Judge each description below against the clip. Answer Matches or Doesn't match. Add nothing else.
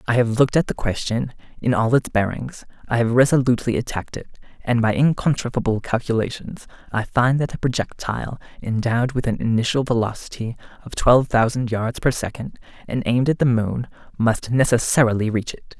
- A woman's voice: Doesn't match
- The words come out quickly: Doesn't match